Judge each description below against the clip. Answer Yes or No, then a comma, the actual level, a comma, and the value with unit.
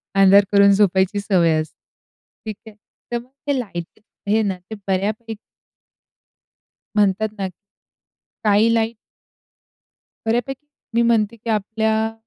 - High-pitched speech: Yes, high, 215 Hz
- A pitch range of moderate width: No, narrow, 2.2 semitones